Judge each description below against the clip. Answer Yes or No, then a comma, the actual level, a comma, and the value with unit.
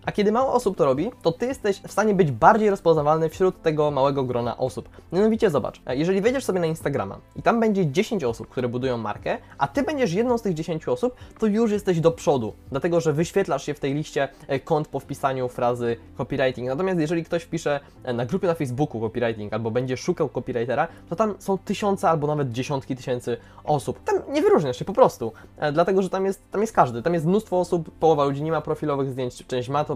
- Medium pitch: Yes, medium, 160 Hz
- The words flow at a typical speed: No, fast, 215 wpm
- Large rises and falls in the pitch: Yes, wide, 6.8 semitones